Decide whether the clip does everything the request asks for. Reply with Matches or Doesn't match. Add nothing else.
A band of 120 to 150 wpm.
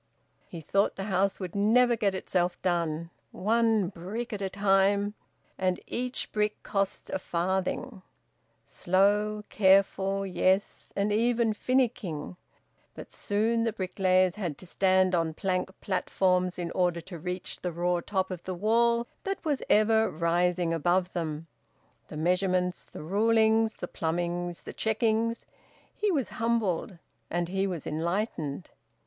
Matches